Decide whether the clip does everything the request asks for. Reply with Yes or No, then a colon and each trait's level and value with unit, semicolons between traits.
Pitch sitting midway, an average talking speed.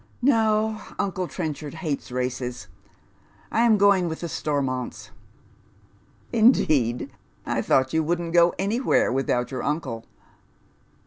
No: medium, 160 Hz; slow, 130 wpm